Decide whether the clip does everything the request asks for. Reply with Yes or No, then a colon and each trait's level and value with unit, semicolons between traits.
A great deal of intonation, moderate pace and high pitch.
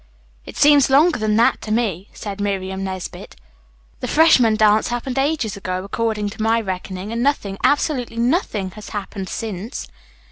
No: average, 3.7 semitones; average, 155 wpm; high, 215 Hz